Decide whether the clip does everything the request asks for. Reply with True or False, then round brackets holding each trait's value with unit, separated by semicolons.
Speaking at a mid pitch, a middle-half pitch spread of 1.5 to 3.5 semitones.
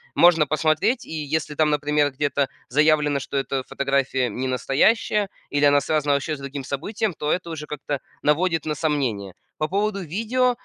True (150 Hz; 2.9 semitones)